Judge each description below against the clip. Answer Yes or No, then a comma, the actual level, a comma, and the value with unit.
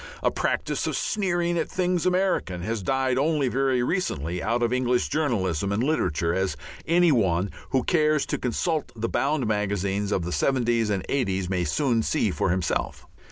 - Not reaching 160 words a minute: No, average, 170 wpm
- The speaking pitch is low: Yes, low, 120 Hz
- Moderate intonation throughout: No, wide, 7.7 semitones